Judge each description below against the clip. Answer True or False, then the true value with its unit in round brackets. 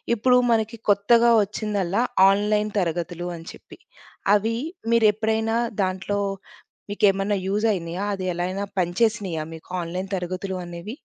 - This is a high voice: True (200 Hz)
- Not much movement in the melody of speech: False (3.2 semitones)